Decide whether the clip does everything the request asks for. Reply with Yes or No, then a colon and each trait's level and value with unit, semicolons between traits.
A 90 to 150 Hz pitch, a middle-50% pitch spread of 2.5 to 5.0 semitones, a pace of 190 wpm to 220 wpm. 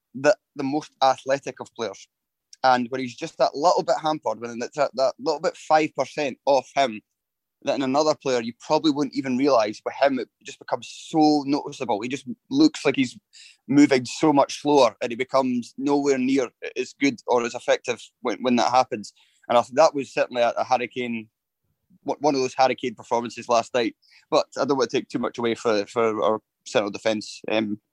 Yes: low, 135 Hz; average, 4.3 semitones; average, 200 wpm